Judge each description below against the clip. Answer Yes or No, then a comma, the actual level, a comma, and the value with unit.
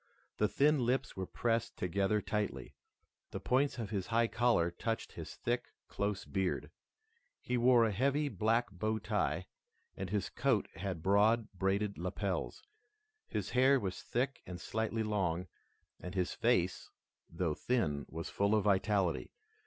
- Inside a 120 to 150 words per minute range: Yes, average, 145 wpm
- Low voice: Yes, low, 105 Hz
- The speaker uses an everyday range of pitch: Yes, average, 3.8 semitones